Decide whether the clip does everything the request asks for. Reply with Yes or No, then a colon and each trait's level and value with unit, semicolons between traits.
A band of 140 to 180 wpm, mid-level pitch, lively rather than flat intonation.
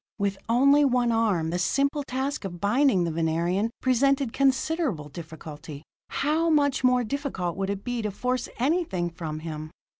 No: average, 155 wpm; high, 225 Hz; wide, 8.0 semitones